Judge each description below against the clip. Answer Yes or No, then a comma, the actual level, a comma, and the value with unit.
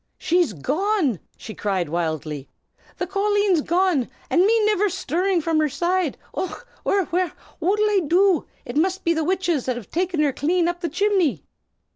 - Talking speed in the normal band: Yes, average, 160 wpm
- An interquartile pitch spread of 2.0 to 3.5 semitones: No, average, 5.0 semitones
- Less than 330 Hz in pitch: No, very high, 350 Hz